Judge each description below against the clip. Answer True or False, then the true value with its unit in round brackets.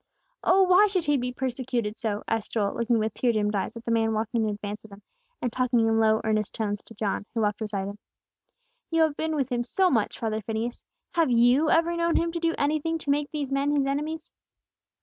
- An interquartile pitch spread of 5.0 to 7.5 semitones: True (5.4 semitones)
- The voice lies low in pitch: False (240 Hz)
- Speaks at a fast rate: True (230 wpm)